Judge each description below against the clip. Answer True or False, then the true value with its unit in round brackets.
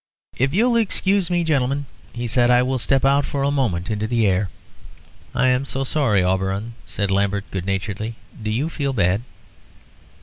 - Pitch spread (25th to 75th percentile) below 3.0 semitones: False (5.5 semitones)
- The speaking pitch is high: False (120 Hz)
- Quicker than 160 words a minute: True (170 wpm)